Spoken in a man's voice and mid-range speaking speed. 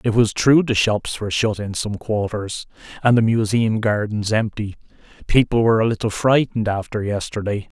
Yes: male; average, 170 wpm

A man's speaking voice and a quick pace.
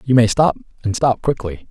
Yes: male; fast, 210 wpm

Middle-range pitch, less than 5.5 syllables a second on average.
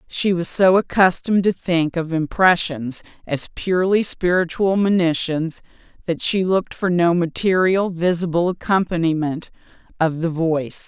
Yes: medium, 175 Hz; 4.6 syllables/s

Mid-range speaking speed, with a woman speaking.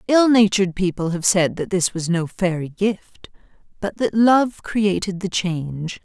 Yes: average, 170 wpm; female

